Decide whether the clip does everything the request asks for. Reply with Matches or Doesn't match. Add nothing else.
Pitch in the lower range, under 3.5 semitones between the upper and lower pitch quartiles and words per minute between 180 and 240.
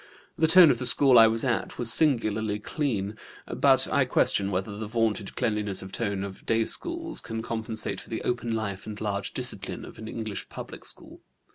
Matches